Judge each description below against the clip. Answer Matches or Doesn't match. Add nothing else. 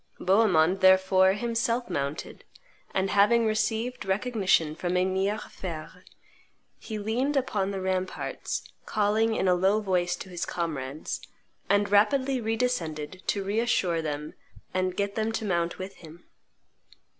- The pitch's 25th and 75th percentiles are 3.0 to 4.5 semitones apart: Matches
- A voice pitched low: Doesn't match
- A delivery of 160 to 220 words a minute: Doesn't match